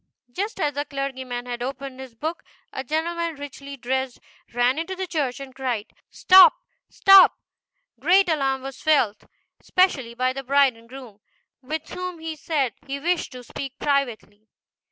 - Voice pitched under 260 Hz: No, very high, 275 Hz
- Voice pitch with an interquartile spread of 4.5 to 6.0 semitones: No, average, 4.0 semitones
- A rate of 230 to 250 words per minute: No, average, 165 wpm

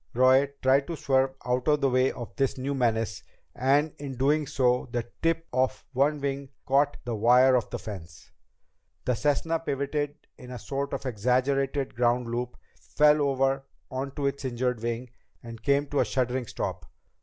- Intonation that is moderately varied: No, narrow, 2.2 semitones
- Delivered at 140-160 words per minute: No, average, 170 wpm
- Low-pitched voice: Yes, low, 130 Hz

